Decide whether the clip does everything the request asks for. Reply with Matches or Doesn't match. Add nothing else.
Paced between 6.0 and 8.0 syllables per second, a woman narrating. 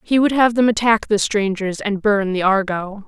Doesn't match